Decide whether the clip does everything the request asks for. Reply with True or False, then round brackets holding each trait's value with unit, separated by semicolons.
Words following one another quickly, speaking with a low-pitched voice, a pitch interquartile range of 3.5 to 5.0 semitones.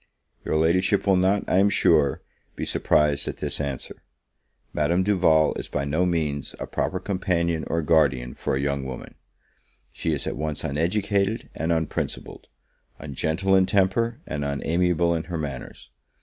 False (155 wpm; 80 Hz; 4.5 semitones)